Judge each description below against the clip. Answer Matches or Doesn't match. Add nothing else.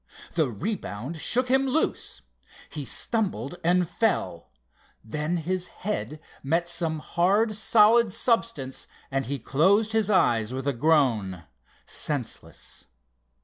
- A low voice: Doesn't match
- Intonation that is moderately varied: Doesn't match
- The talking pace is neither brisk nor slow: Doesn't match